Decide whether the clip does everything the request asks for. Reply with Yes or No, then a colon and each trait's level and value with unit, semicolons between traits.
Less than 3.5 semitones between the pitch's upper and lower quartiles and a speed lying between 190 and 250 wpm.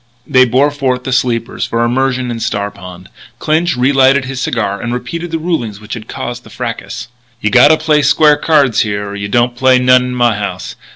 Yes: average, 2.9 semitones; fast, 205 wpm